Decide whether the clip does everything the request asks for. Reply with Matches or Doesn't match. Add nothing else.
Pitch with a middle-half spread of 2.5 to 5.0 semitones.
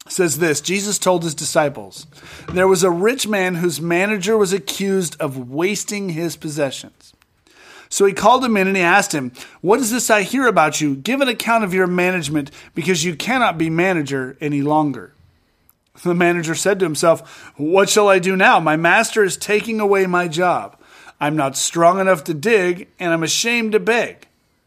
Matches